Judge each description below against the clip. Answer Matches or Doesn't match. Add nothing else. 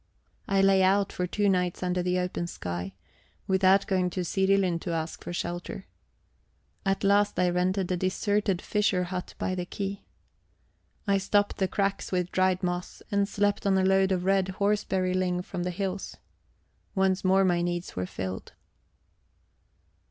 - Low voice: Doesn't match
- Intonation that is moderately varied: Doesn't match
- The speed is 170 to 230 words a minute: Doesn't match